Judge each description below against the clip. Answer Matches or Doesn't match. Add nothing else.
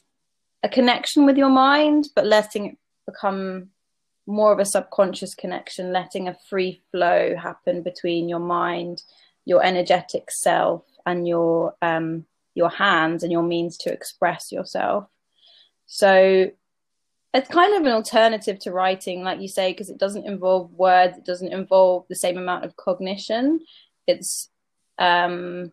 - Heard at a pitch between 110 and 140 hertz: Doesn't match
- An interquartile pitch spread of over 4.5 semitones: Doesn't match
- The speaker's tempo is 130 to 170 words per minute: Matches